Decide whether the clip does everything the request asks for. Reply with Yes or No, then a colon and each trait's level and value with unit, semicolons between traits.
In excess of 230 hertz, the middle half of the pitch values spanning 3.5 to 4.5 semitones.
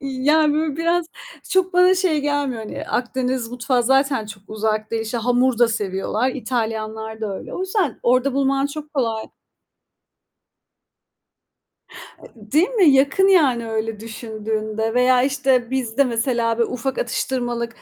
Yes: very high, 250 Hz; average, 3.9 semitones